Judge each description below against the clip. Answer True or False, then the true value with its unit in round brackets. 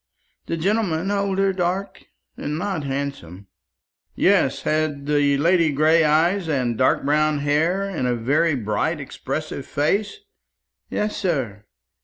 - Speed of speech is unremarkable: False (125 wpm)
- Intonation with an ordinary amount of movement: True (4.5 semitones)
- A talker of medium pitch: True (155 Hz)